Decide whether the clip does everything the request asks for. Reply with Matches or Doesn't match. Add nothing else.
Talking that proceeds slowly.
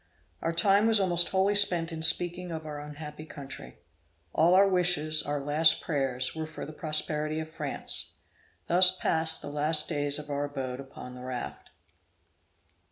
Doesn't match